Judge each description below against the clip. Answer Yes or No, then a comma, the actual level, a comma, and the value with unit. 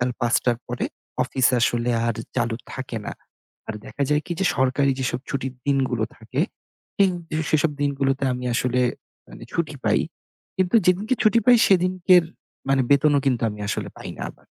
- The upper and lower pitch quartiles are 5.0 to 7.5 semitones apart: Yes, average, 5.3 semitones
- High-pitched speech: No, low, 135 Hz